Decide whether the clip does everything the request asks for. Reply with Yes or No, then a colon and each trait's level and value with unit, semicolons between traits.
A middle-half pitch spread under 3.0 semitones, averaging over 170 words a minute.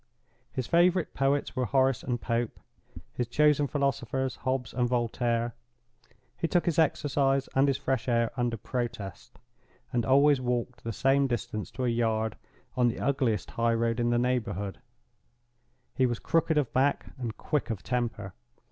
No: narrow, 2.6 semitones; average, 155 wpm